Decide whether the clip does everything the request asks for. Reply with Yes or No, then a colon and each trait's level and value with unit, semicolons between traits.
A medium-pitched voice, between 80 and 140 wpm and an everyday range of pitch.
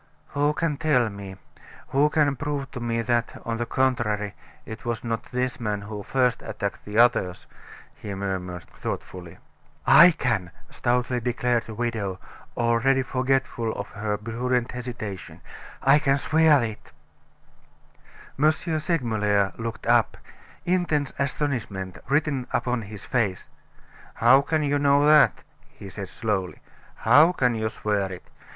No: low, 120 Hz; slow, 135 wpm; average, 4.7 semitones